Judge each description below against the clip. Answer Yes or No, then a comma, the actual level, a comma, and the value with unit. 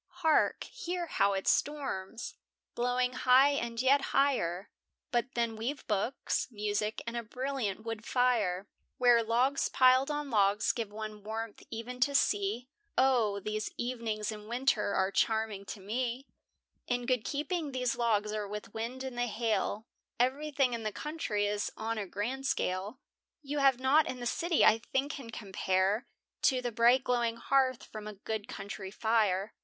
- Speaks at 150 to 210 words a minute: Yes, average, 160 wpm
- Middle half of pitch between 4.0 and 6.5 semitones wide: No, average, 3.5 semitones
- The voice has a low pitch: No, high, 235 Hz